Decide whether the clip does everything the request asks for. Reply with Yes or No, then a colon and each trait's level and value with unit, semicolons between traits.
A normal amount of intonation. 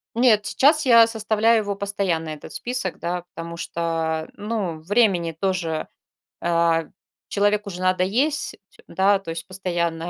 Yes: average, 4.0 semitones